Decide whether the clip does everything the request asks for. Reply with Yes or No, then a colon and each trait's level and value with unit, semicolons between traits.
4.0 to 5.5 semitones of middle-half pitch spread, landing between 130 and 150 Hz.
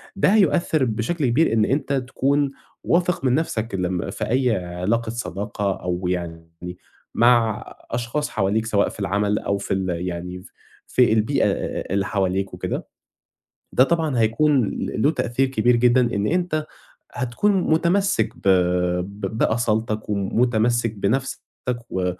No: average, 5.2 semitones; low, 115 Hz